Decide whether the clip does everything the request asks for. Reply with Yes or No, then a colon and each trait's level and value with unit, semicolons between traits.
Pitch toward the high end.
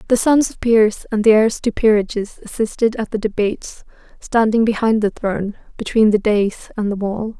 Yes: high, 215 Hz